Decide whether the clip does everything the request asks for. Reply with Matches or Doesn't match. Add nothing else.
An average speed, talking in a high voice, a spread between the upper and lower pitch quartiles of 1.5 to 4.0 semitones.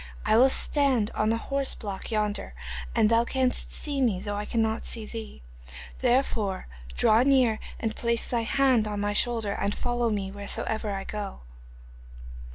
Matches